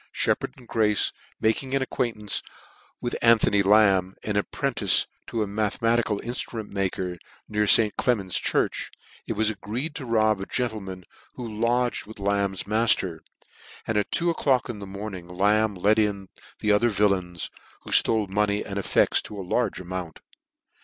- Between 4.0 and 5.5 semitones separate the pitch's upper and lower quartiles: No, average, 2.7 semitones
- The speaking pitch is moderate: No, low, 105 Hz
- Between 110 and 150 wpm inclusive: No, average, 160 wpm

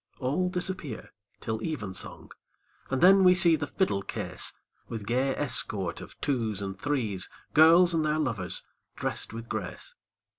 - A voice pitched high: No, low, 135 Hz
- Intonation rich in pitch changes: Yes, wide, 7.1 semitones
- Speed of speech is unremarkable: Yes, average, 145 wpm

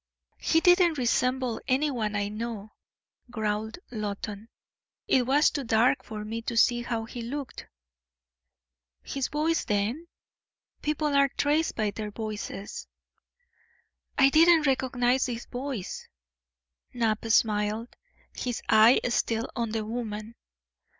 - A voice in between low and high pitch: No, high, 235 Hz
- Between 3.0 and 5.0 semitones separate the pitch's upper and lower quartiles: Yes, average, 3.8 semitones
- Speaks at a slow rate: Yes, slow, 115 wpm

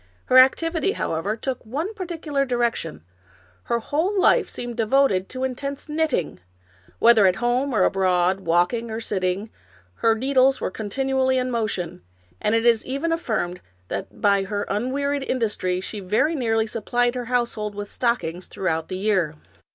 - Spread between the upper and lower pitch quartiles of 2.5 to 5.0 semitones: No, wide, 5.4 semitones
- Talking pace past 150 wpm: Yes, average, 160 wpm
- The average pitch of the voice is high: Yes, high, 230 Hz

